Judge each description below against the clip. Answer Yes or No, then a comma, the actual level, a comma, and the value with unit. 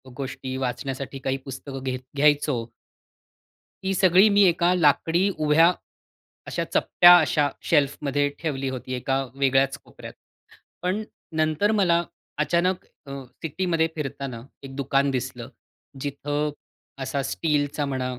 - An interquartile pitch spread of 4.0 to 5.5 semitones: No, average, 3.6 semitones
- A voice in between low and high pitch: Yes, medium, 145 Hz